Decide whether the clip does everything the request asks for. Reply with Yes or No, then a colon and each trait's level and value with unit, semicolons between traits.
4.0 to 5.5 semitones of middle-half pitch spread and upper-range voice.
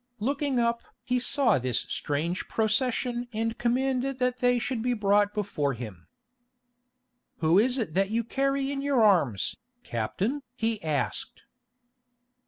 Yes: average, 5.1 semitones; high, 230 Hz